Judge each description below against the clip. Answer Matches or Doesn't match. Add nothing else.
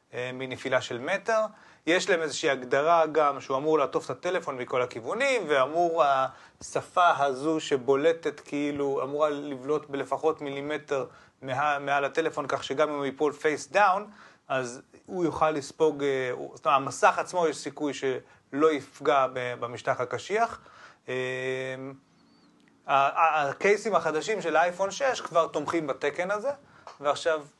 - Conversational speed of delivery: Matches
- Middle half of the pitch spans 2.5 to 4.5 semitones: Matches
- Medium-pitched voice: Matches